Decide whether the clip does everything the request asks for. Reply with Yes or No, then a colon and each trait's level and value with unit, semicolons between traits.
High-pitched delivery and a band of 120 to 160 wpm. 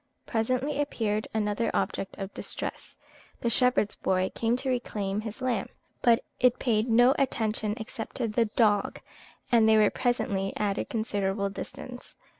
Yes: high, 220 Hz; average, 150 wpm